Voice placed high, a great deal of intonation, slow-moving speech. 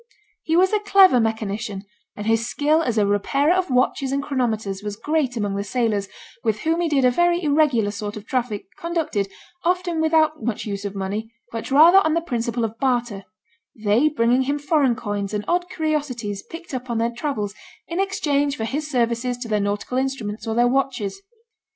No: high, 245 Hz; wide, 6.1 semitones; average, 190 wpm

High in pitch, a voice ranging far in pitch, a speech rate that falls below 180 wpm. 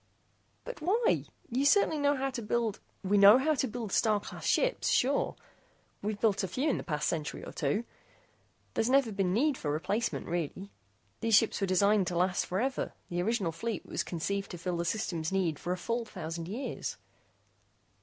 No: high, 205 Hz; wide, 5.8 semitones; average, 190 wpm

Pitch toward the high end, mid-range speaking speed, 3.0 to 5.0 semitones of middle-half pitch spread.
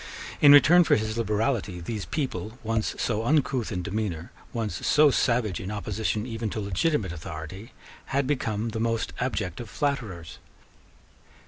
No: low, 110 Hz; average, 145 wpm; average, 3.7 semitones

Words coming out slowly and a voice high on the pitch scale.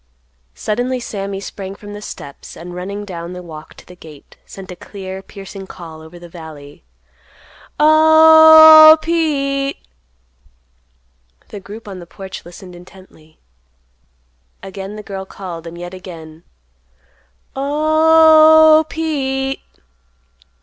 Yes: slow, 115 wpm; high, 195 Hz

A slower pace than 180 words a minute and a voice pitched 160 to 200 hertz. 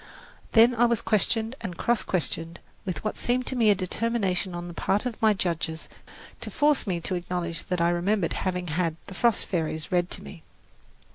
No: average, 195 wpm; medium, 185 Hz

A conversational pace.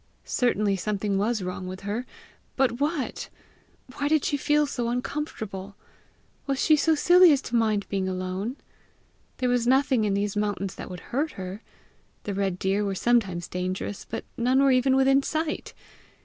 Yes: average, 165 wpm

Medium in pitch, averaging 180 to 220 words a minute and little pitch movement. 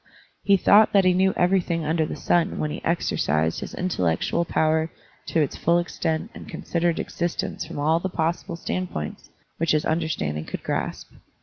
No: medium, 165 Hz; average, 170 wpm; narrow, 2.2 semitones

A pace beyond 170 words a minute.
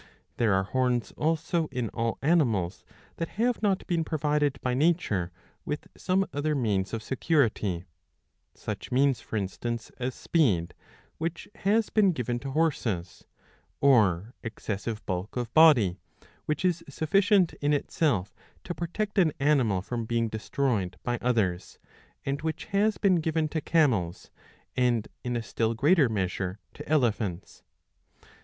No: average, 140 wpm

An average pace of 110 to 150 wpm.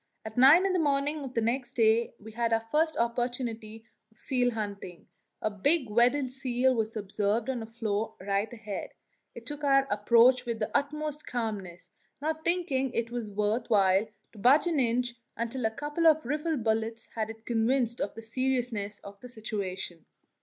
No: average, 175 wpm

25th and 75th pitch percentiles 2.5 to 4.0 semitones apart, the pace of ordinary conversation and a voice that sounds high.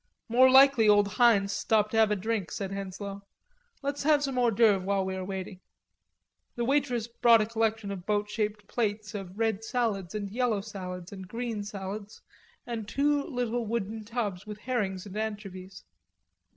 Yes: average, 3.0 semitones; average, 170 wpm; high, 215 Hz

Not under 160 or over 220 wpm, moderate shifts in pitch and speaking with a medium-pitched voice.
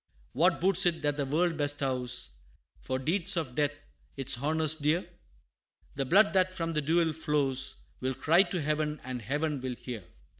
Yes: average, 165 wpm; average, 3.7 semitones; medium, 150 Hz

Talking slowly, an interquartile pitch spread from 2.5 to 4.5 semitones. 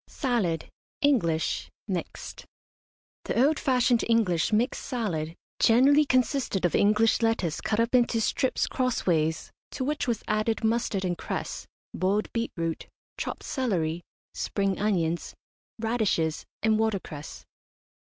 No: slow, 115 wpm; wide, 5.6 semitones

